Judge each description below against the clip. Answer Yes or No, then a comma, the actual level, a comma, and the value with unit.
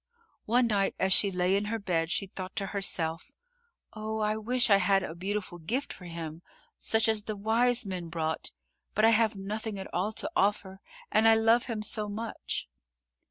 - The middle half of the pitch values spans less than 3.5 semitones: Yes, average, 2.9 semitones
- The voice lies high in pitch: Yes, high, 205 Hz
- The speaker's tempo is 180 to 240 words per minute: Yes, average, 190 wpm